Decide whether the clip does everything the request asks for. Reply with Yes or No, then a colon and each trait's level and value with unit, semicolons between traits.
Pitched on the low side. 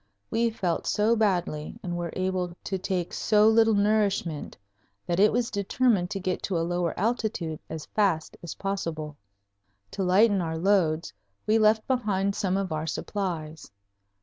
No: high, 190 Hz